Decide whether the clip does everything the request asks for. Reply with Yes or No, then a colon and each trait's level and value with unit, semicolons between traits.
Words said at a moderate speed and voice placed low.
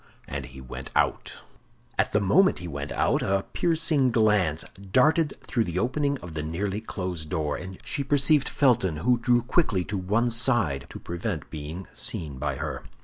Yes: average, 175 wpm; low, 100 Hz